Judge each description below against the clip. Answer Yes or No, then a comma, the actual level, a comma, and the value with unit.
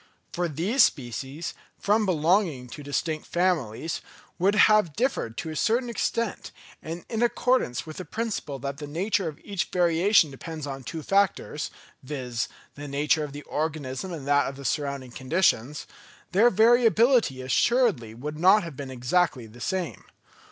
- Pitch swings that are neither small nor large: No, wide, 6.1 semitones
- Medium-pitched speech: Yes, medium, 160 Hz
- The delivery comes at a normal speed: Yes, average, 155 wpm